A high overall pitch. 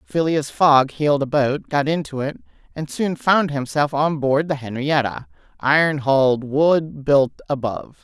No: medium, 145 Hz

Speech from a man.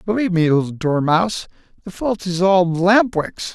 Yes: male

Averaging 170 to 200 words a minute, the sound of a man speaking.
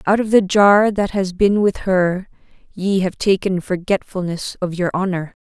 No: average, 175 wpm; female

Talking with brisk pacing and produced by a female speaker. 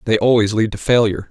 No: fast, 230 wpm; male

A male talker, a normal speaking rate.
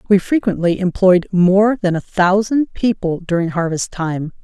No: female; average, 150 wpm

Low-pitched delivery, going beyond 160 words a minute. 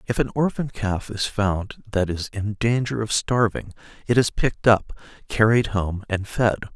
Yes: low, 110 Hz; average, 180 wpm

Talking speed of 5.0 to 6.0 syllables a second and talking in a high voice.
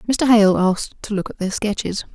Yes: 5.7 syllables/s; high, 205 Hz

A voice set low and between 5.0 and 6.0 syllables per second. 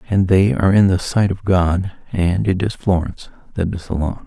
Yes: very low, 95 Hz; 5.3 syllables/s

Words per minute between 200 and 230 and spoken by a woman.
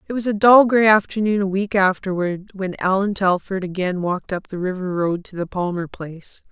Yes: fast, 205 wpm; female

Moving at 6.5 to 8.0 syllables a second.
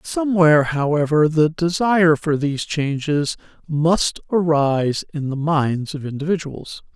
No: 4.5 syllables/s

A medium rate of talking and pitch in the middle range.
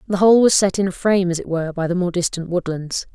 No: fast, 285 wpm; medium, 180 Hz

